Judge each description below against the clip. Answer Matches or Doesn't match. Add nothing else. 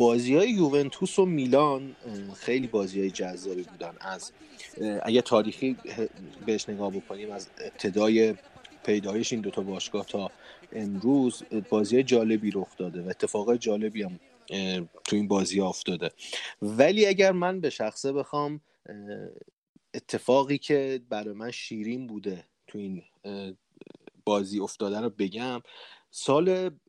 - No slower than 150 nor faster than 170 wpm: Doesn't match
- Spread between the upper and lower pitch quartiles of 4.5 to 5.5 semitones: Matches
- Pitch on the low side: Matches